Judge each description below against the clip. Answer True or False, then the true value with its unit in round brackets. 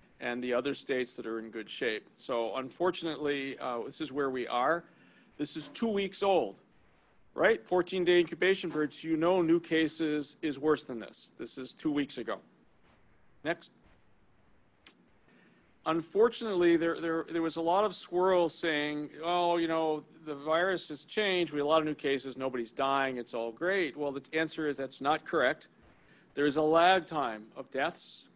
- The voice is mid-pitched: True (155 Hz)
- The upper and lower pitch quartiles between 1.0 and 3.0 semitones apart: False (3.8 semitones)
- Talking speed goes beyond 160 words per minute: True (180 wpm)